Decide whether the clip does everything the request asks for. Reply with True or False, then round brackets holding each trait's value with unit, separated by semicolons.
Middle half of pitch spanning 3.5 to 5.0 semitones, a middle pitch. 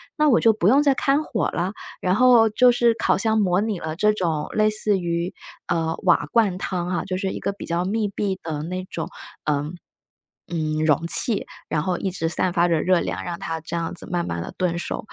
True (4.1 semitones; 180 Hz)